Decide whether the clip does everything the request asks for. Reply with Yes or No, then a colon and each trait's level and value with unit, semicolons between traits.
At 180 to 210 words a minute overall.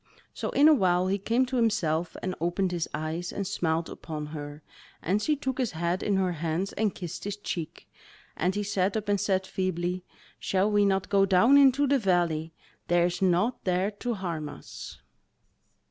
Yes: average, 190 wpm